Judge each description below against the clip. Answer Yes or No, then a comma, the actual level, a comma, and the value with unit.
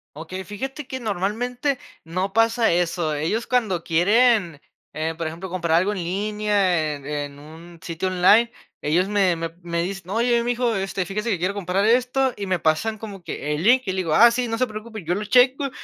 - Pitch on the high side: Yes, high, 195 Hz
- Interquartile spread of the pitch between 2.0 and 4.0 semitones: No, average, 5.1 semitones